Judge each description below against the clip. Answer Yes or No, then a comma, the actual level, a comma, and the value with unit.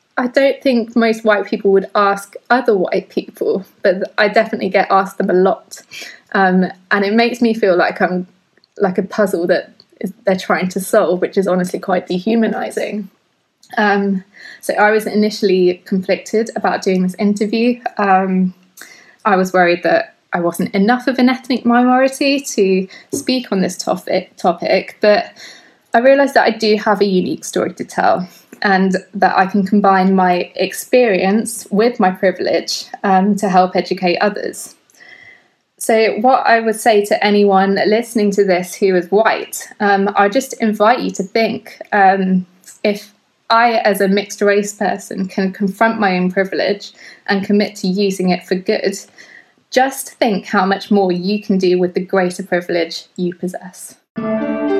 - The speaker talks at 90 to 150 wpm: No, average, 165 wpm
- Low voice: No, high, 200 Hz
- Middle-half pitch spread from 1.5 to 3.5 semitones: Yes, average, 2.9 semitones